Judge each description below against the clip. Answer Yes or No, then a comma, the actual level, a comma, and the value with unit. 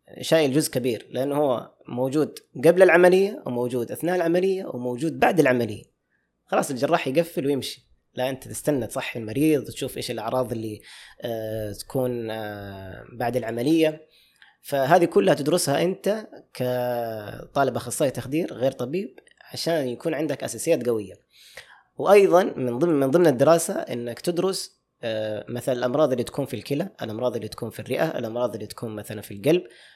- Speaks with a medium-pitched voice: No, low, 130 Hz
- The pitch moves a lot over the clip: Yes, wide, 5.7 semitones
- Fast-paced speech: Yes, fast, 145 wpm